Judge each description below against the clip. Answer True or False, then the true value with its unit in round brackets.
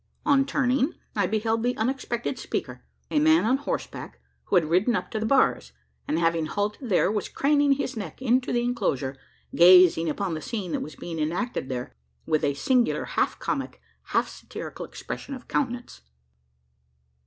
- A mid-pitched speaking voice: False (220 Hz)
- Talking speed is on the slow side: False (165 wpm)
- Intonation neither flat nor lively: False (7.4 semitones)